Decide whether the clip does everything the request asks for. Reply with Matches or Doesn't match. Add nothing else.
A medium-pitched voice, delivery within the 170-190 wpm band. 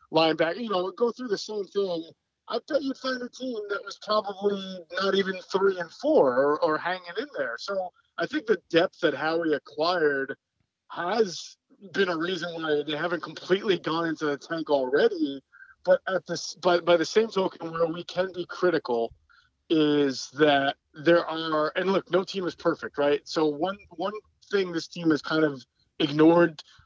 Matches